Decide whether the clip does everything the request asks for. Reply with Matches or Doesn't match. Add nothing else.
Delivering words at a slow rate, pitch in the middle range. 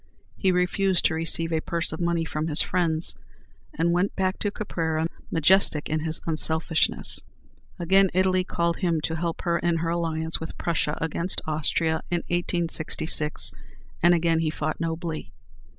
Doesn't match